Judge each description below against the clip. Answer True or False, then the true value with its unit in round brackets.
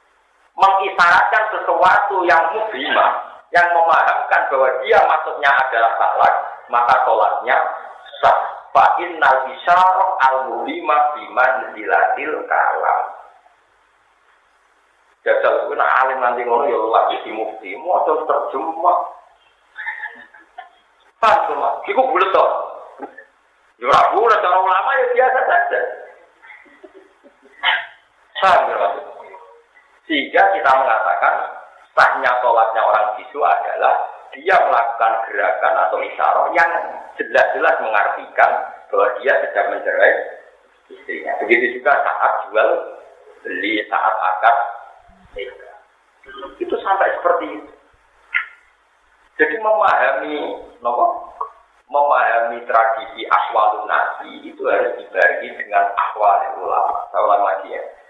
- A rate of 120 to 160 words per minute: False (95 wpm)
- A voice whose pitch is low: False (340 Hz)